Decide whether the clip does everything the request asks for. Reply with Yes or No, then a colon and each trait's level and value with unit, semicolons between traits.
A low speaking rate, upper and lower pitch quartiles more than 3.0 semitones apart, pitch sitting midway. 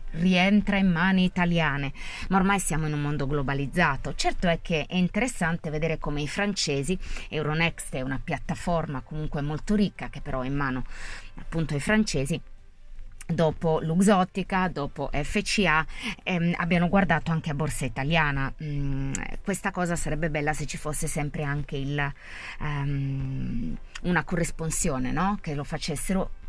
No: average, 145 wpm; average, 4.0 semitones; medium, 155 Hz